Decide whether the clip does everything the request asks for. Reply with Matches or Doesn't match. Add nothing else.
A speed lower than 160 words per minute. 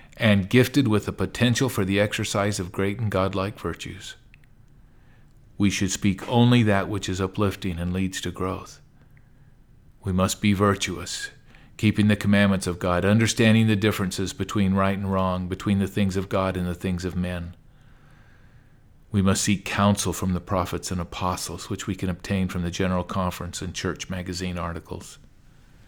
Doesn't match